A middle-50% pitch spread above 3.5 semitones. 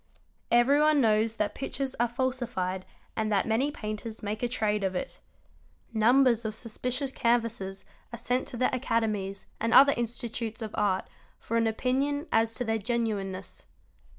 No: average, 2.8 semitones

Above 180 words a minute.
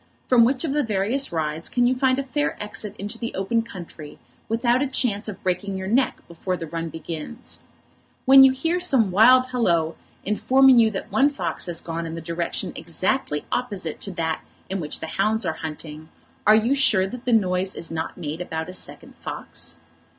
Yes: average, 195 wpm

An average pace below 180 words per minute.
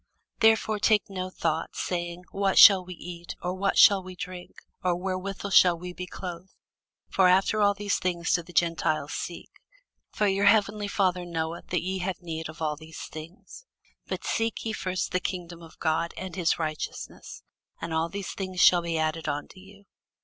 No: average, 185 wpm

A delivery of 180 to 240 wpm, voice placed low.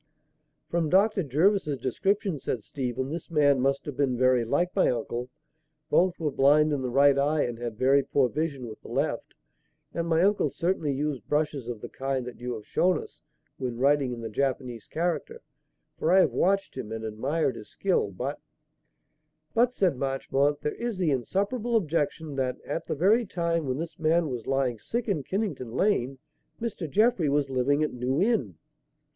No: average, 185 wpm; medium, 145 Hz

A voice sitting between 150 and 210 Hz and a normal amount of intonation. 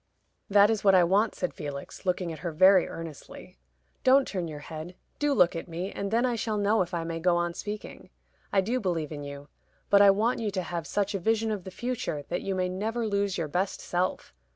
Yes: medium, 185 Hz; average, 3.6 semitones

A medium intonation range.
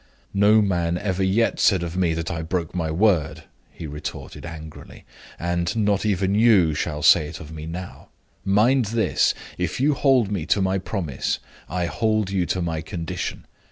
Yes: average, 3.9 semitones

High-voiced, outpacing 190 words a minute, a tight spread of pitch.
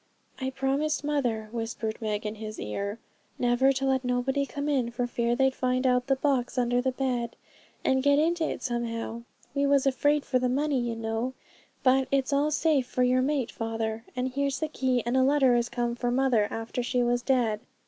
Yes: very high, 255 Hz; average, 200 wpm; narrow, 2.3 semitones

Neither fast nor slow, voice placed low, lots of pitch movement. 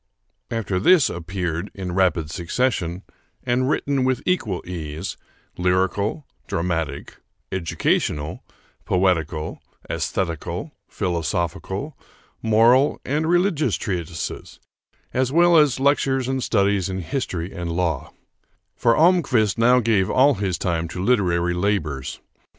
No: slow, 110 wpm; very low, 95 Hz; wide, 6.9 semitones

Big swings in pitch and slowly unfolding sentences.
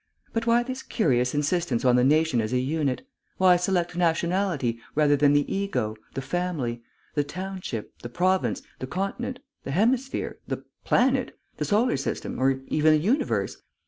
No: wide, 6.4 semitones; average, 160 wpm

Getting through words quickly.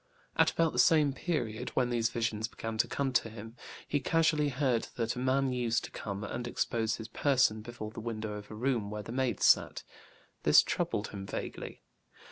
No: average, 195 wpm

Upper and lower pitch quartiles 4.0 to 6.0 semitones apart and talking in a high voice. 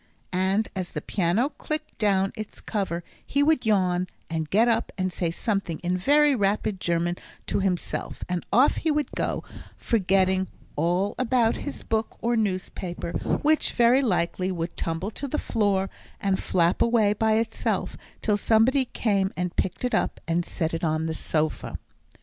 Yes: average, 4.4 semitones; high, 195 Hz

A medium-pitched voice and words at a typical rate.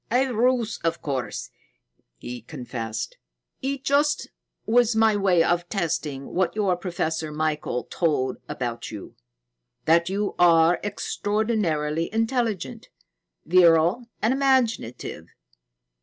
No: medium, 175 Hz; slow, 105 wpm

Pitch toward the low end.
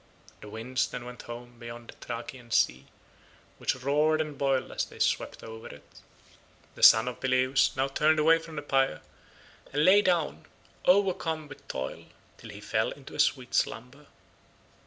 Yes: low, 130 Hz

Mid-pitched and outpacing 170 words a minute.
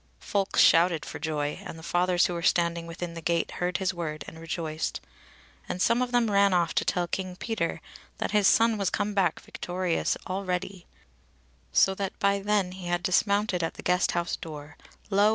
Yes: medium, 180 Hz; average, 190 wpm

